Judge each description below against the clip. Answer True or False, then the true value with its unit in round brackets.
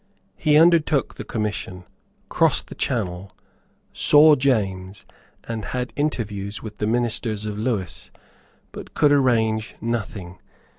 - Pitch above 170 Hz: False (110 Hz)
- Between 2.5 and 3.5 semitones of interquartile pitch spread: False (4.3 semitones)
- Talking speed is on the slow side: True (115 wpm)